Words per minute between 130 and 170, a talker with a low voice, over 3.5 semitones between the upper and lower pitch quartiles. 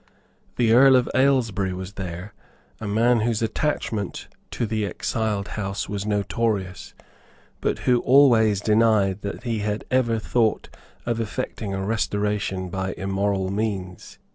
No: slow, 135 wpm; low, 105 Hz; average, 2.8 semitones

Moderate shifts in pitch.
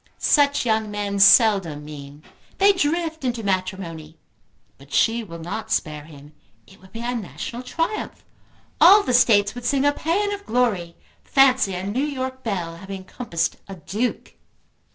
No: wide, 6.8 semitones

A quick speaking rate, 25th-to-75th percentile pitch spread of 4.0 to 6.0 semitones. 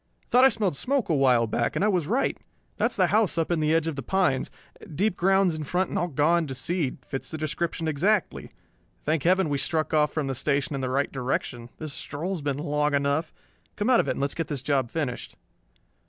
Yes: fast, 230 wpm; average, 4.5 semitones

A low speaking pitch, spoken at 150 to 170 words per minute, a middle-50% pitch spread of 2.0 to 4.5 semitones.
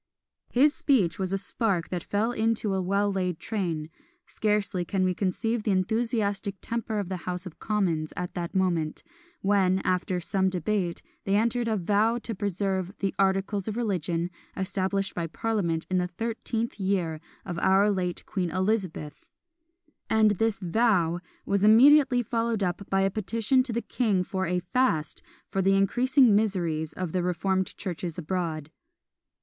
No: high, 195 Hz; average, 160 wpm; average, 3.4 semitones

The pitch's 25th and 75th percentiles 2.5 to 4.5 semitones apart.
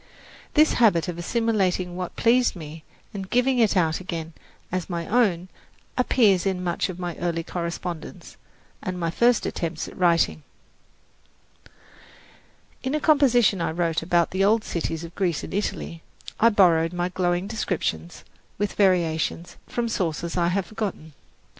Yes: average, 3.8 semitones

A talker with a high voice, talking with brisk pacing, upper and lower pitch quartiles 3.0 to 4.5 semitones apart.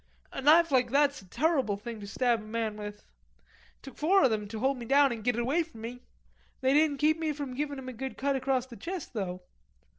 Yes: very high, 260 Hz; fast, 245 wpm; average, 4.2 semitones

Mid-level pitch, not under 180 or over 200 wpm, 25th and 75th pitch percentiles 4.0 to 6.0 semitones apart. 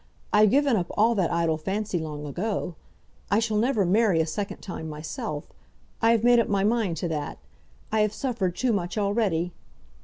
No: high, 200 Hz; average, 185 wpm; average, 4.7 semitones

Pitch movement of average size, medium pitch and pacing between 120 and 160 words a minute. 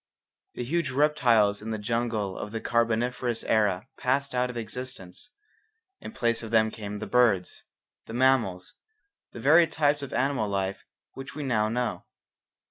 No: average, 3.4 semitones; low, 115 Hz; average, 155 wpm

